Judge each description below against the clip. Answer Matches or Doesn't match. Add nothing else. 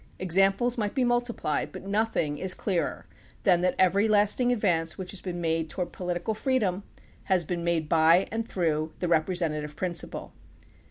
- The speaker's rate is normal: Matches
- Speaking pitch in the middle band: Matches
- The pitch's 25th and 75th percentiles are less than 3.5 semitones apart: Doesn't match